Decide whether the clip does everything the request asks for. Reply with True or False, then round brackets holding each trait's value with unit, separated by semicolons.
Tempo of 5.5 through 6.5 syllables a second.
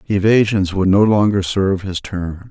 False (4.6 syllables/s)